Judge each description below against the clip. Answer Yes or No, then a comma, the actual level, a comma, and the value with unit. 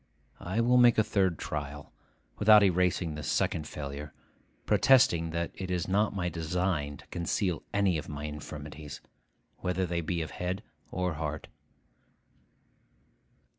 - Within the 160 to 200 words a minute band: No, slow, 135 wpm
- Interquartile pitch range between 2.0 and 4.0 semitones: Yes, average, 3.7 semitones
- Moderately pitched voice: No, very low, 85 Hz